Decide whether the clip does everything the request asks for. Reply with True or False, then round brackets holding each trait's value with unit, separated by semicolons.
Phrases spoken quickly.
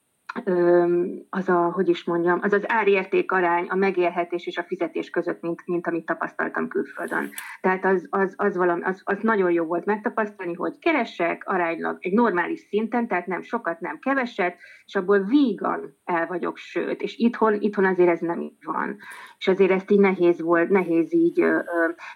True (180 wpm)